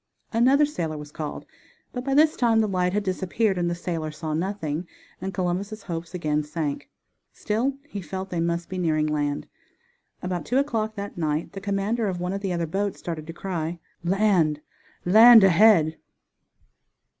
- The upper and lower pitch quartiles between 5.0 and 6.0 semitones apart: No, average, 4.2 semitones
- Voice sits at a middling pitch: Yes, medium, 180 Hz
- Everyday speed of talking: Yes, average, 170 wpm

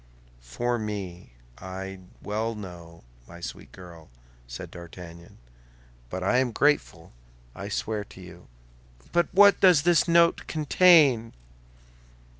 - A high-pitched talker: No, low, 105 Hz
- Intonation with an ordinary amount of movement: No, wide, 8.4 semitones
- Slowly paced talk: Yes, slow, 115 wpm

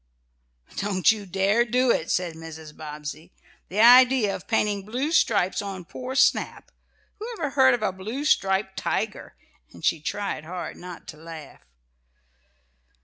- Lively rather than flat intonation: Yes, wide, 6.4 semitones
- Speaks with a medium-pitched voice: No, high, 195 Hz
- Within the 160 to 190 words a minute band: No, average, 145 wpm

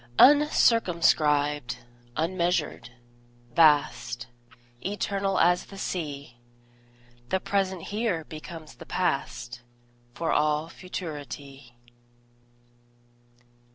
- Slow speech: Yes, slow, 70 wpm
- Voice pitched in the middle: Yes, medium, 165 Hz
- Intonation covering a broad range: No, average, 4.4 semitones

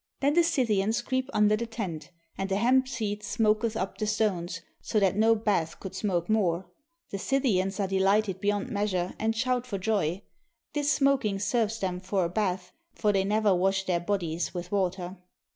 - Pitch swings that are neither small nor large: Yes, average, 3.0 semitones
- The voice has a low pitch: No, high, 205 Hz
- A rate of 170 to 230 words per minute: Yes, average, 185 wpm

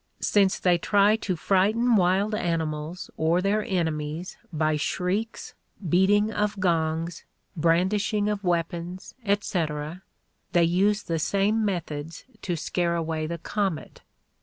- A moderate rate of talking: No, slow, 120 wpm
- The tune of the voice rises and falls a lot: No, average, 3.7 semitones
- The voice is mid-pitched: Yes, medium, 180 Hz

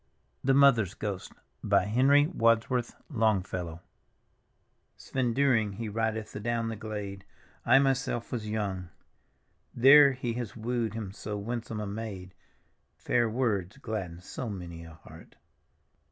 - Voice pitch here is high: No, low, 110 Hz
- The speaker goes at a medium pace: No, slow, 125 wpm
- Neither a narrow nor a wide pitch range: Yes, average, 3.5 semitones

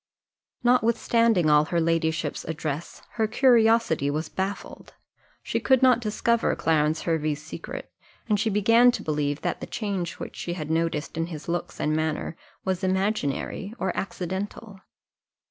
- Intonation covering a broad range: Yes, wide, 5.7 semitones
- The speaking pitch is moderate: Yes, medium, 180 Hz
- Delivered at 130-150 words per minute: Yes, average, 145 wpm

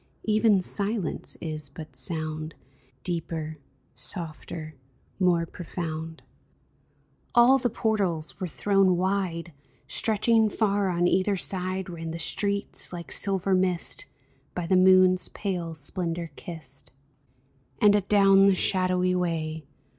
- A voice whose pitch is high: No, medium, 180 Hz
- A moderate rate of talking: No, slow, 110 wpm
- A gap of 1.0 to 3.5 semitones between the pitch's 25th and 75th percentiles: Yes, average, 3.1 semitones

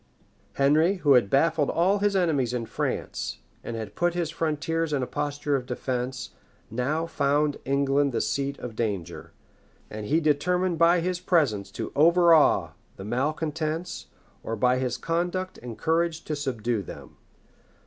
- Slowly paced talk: No, average, 155 wpm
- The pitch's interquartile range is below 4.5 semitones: No, average, 4.9 semitones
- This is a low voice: No, medium, 145 Hz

